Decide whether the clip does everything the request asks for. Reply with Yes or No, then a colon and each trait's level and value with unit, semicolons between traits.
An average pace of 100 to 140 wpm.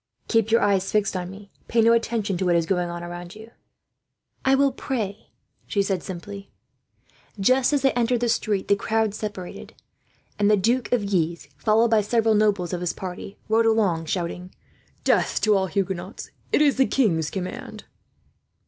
No: average, 175 wpm